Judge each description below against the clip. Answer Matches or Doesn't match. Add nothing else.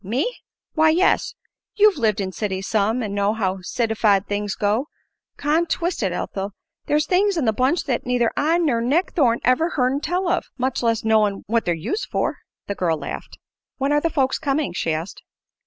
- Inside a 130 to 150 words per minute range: Doesn't match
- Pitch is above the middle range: Matches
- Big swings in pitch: Matches